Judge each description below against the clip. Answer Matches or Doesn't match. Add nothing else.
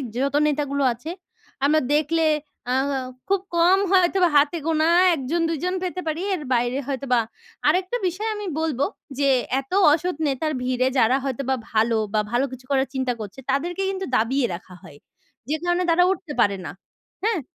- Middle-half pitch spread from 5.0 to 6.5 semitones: Matches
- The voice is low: Doesn't match